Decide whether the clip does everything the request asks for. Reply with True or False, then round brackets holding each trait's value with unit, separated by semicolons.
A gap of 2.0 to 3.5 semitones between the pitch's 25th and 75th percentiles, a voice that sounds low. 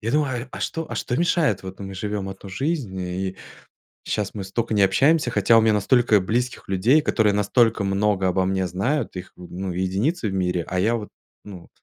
False (4.3 semitones; 105 Hz)